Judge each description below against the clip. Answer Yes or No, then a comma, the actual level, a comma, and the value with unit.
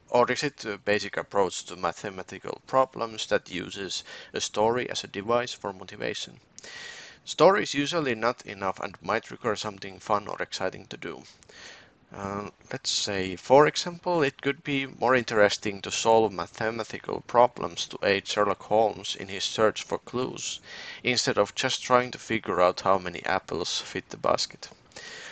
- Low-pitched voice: Yes, low, 110 Hz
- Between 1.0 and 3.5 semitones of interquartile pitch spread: No, average, 3.9 semitones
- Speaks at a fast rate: Yes, fast, 160 wpm